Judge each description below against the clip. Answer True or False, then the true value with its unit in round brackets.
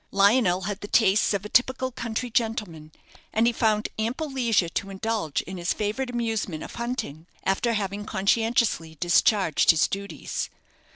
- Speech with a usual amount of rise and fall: True (3.4 semitones)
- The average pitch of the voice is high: True (210 Hz)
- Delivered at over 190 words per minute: False (155 wpm)